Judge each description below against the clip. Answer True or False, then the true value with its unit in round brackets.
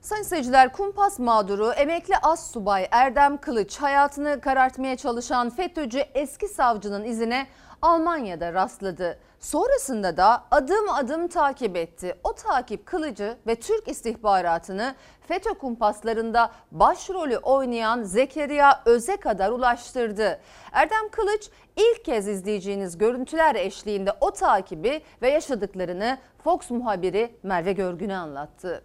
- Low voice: False (255 Hz)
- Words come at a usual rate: True (110 wpm)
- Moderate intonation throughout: False (6.8 semitones)